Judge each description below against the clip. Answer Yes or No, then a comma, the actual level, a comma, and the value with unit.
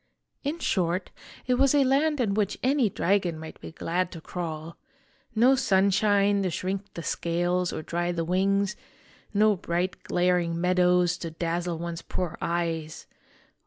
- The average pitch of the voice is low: No, medium, 180 Hz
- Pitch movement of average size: Yes, average, 3.1 semitones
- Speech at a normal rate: Yes, average, 150 wpm